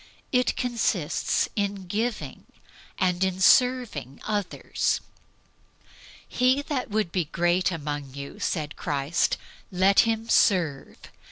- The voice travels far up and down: Yes, wide, 6.2 semitones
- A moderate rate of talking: No, slow, 105 wpm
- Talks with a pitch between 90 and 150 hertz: No, high, 190 Hz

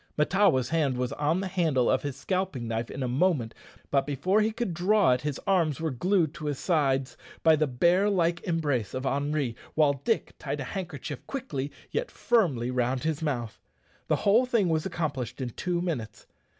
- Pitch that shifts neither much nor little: No, wide, 5.7 semitones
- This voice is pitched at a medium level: Yes, medium, 150 Hz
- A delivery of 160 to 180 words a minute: No, average, 190 wpm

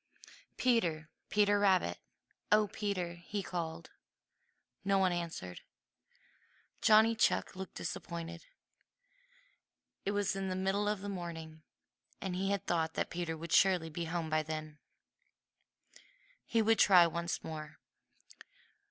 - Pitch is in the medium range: Yes, medium, 175 Hz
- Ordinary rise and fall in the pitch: Yes, average, 3.6 semitones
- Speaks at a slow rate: Yes, slow, 120 wpm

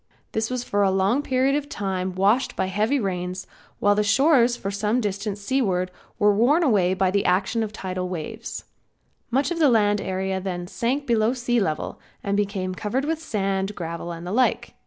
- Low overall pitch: No, high, 205 Hz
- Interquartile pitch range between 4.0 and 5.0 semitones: Yes, average, 4.4 semitones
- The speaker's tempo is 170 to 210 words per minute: Yes, average, 190 wpm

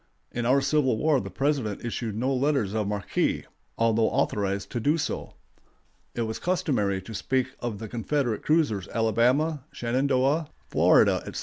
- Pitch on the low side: Yes, low, 120 Hz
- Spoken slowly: No, average, 150 wpm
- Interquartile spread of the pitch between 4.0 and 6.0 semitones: Yes, average, 4.4 semitones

